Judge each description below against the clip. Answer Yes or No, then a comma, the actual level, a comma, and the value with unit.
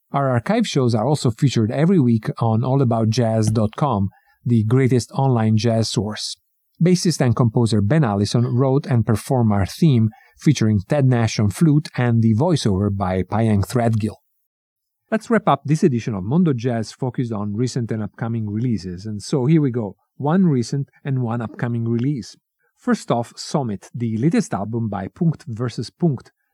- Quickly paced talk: No, average, 160 wpm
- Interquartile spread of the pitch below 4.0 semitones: No, average, 4.3 semitones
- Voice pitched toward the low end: Yes, low, 120 Hz